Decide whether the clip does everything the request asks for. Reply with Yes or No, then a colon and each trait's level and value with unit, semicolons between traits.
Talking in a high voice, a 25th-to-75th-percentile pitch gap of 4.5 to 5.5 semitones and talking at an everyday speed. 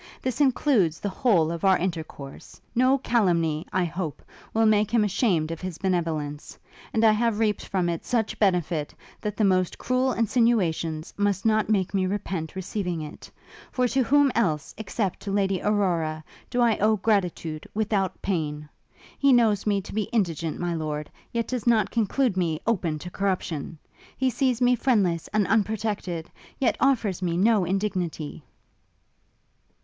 Yes: high, 195 Hz; average, 4.8 semitones; average, 160 wpm